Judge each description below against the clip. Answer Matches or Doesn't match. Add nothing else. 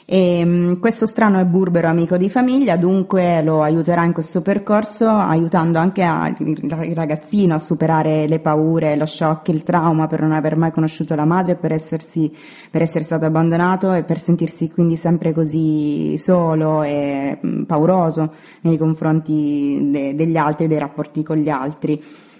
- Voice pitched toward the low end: Doesn't match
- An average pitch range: Doesn't match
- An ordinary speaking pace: Matches